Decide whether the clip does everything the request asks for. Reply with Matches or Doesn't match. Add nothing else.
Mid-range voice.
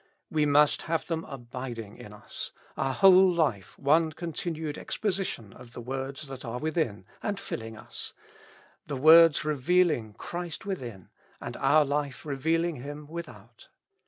Matches